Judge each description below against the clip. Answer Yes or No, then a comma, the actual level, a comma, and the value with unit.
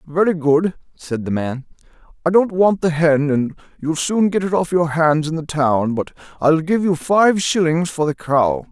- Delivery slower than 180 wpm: No, fast, 205 wpm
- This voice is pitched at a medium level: Yes, medium, 160 Hz